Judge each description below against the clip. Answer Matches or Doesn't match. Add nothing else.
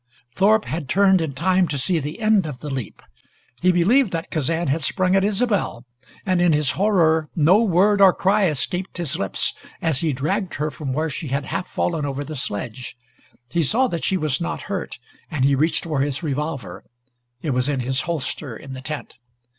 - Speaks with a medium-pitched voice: Matches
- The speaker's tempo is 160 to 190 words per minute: Doesn't match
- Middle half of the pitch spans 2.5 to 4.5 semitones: Doesn't match